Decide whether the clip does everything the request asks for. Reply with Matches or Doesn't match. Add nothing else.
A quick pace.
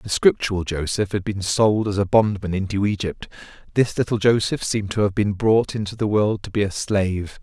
Matches